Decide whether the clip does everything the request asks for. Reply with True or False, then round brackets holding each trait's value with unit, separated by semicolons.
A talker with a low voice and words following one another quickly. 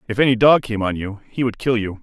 True (115 Hz; 295 wpm)